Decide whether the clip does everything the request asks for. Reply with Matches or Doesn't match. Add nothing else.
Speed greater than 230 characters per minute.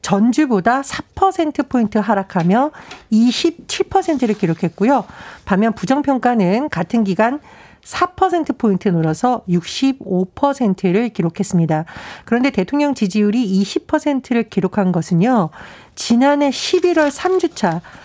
Doesn't match